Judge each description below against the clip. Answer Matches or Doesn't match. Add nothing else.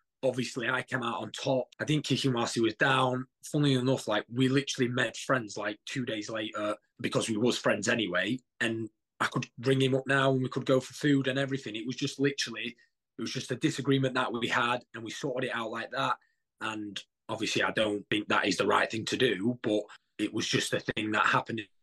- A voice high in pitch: Doesn't match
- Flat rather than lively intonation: Doesn't match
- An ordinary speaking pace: Doesn't match